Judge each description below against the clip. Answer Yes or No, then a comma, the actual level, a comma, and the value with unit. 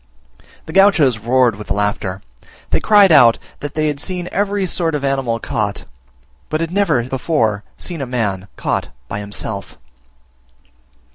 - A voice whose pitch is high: No, low, 135 Hz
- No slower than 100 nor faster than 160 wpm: Yes, average, 145 wpm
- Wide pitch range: Yes, wide, 7.5 semitones